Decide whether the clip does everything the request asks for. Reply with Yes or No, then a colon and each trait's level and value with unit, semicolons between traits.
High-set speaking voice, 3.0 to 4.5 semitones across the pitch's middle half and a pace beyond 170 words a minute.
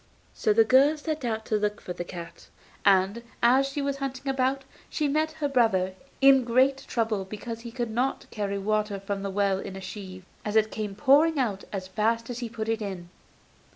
No: high, 225 Hz; average, 5.1 semitones; fast, 205 wpm